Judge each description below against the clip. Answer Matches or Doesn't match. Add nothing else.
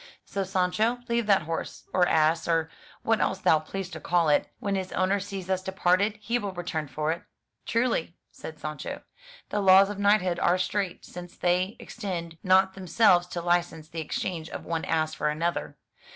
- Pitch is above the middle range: Doesn't match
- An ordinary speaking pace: Matches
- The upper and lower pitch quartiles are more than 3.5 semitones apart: Doesn't match